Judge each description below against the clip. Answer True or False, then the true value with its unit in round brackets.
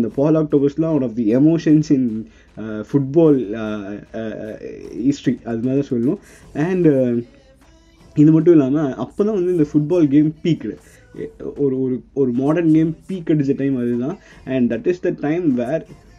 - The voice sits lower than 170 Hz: True (140 Hz)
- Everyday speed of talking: False (150 wpm)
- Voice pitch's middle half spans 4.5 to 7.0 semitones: True (4.9 semitones)